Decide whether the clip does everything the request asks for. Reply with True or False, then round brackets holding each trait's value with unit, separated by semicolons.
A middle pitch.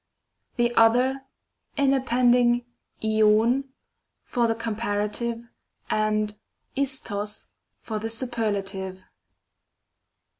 False (230 Hz)